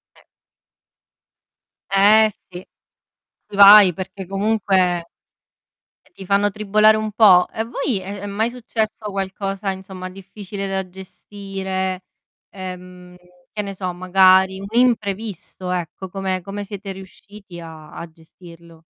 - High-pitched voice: Yes, high, 195 Hz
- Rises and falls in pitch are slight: Yes, narrow, 1.9 semitones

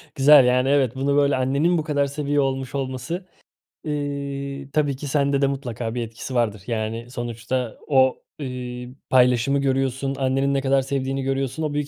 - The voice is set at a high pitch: No, low, 135 Hz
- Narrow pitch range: Yes, narrow, 1.7 semitones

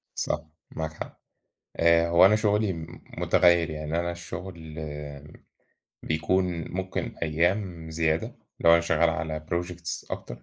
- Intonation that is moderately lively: No, narrow, 2.0 semitones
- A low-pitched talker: Yes, very low, 85 Hz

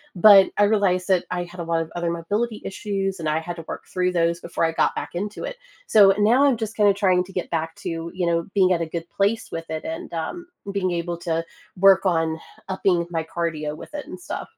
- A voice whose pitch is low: No, medium, 180 Hz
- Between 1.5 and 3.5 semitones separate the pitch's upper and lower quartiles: Yes, average, 3.0 semitones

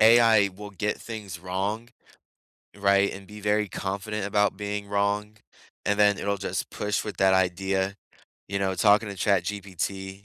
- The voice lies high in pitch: No, low, 100 Hz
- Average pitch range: No, narrow, 1.4 semitones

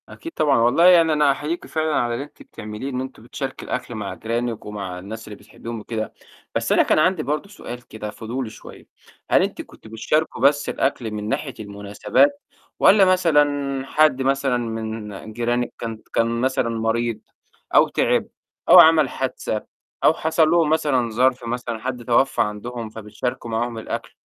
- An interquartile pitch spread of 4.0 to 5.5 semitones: Yes, average, 4.6 semitones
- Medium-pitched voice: No, low, 120 Hz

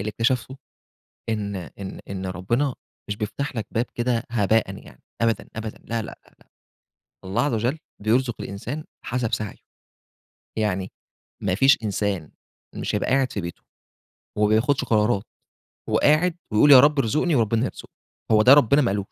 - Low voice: Yes, low, 115 Hz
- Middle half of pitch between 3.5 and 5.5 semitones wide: Yes, average, 4.1 semitones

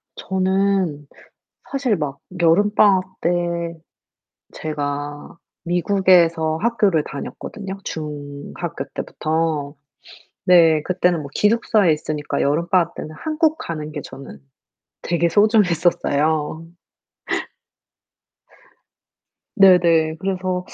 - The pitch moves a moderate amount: Yes, average, 3.9 semitones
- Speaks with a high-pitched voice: No, medium, 170 Hz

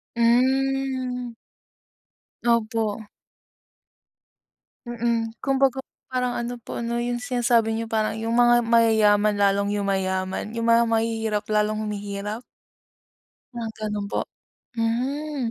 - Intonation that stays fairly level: Yes, narrow, 2.3 semitones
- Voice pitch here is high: Yes, high, 230 Hz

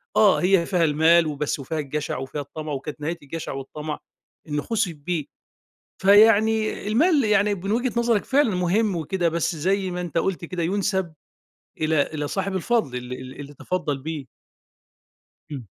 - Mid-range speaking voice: Yes, medium, 170 Hz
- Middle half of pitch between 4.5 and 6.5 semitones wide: Yes, average, 5.1 semitones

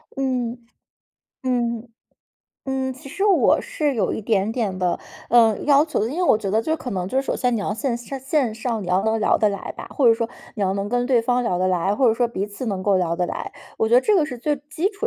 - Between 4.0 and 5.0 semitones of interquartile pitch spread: Yes, average, 4.4 semitones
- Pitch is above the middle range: Yes, high, 235 Hz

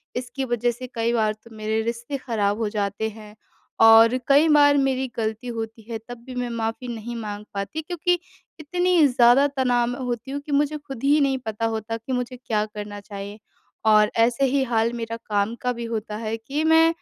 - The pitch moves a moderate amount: Yes, average, 3.4 semitones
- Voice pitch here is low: No, high, 235 Hz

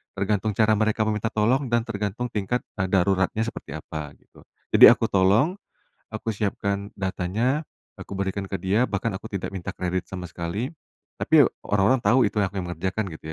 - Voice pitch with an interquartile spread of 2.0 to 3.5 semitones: Yes, average, 2.8 semitones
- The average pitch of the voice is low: Yes, low, 100 Hz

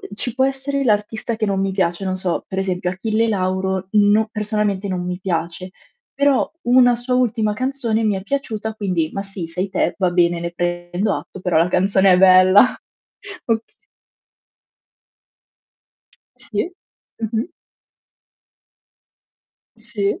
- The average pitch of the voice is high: Yes, high, 200 Hz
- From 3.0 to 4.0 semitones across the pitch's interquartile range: Yes, average, 3.4 semitones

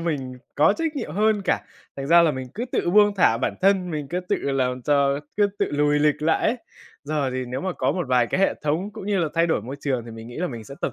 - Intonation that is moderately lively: No, wide, 5.9 semitones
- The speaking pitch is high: No, medium, 150 Hz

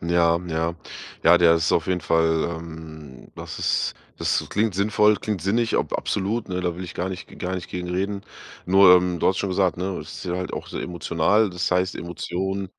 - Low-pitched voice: Yes, very low, 90 Hz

